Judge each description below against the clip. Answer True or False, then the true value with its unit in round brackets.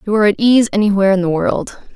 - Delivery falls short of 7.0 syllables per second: False (7.3 syllables/s)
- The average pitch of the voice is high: True (205 Hz)